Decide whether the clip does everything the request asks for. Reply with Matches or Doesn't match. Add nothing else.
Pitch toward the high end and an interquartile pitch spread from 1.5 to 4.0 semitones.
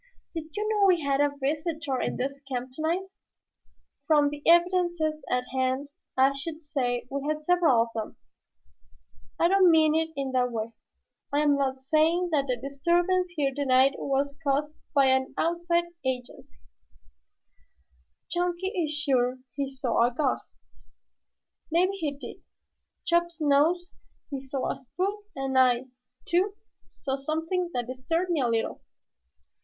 Doesn't match